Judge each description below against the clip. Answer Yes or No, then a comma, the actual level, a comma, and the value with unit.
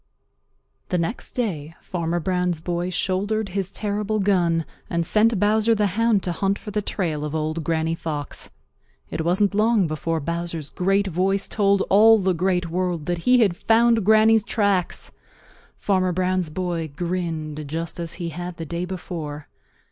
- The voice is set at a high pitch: No, medium, 180 Hz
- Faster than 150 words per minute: Yes, average, 160 wpm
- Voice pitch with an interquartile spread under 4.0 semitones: Yes, average, 3.5 semitones